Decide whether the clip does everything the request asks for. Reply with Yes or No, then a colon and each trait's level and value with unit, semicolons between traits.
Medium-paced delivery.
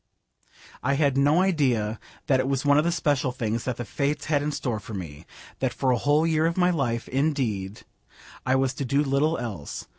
No: fast, 210 wpm